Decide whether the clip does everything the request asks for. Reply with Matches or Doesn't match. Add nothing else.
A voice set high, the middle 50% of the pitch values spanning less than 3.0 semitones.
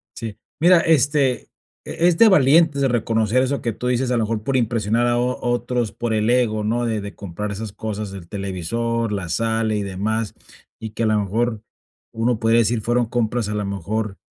Doesn't match